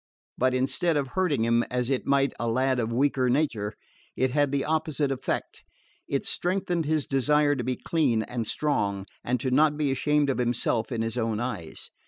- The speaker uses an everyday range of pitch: Yes, average, 3.8 semitones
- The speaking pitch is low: Yes, low, 130 Hz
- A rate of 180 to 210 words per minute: Yes, average, 190 wpm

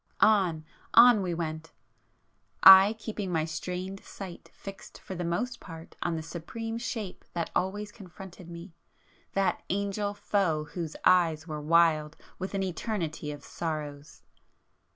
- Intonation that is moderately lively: Yes, average, 3.6 semitones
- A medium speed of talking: No, slow, 125 wpm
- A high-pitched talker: No, medium, 180 Hz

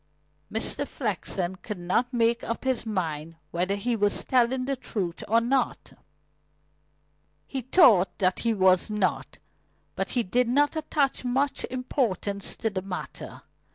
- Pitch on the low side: No, high, 230 Hz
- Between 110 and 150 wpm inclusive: Yes, average, 140 wpm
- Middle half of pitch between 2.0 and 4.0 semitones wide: No, average, 5.1 semitones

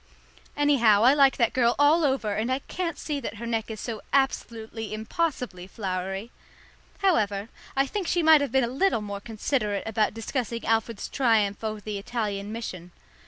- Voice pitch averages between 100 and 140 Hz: No, high, 230 Hz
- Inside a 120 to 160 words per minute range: No, average, 170 wpm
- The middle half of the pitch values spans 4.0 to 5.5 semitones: Yes, average, 4.4 semitones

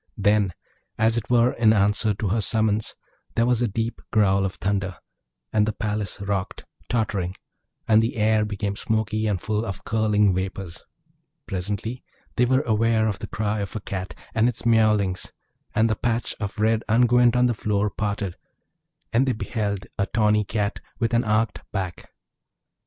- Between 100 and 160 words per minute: No, average, 170 wpm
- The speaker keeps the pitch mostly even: Yes, narrow, 2.0 semitones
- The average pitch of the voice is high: No, low, 105 Hz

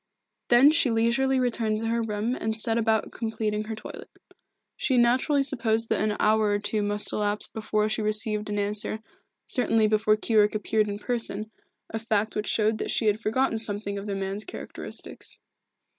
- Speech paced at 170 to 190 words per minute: Yes, average, 175 wpm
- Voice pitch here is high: Yes, high, 220 Hz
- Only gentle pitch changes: Yes, narrow, 1.5 semitones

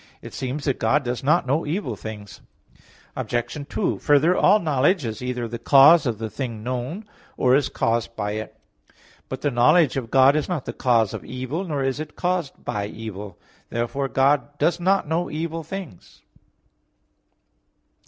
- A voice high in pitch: No, low, 135 Hz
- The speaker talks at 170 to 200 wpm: Yes, average, 175 wpm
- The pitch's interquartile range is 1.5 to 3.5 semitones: No, average, 4.8 semitones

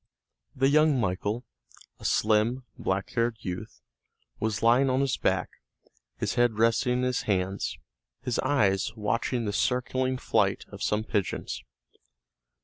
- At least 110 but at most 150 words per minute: Yes, slow, 135 wpm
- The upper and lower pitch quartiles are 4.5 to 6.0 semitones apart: No, average, 3.4 semitones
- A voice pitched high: No, low, 115 Hz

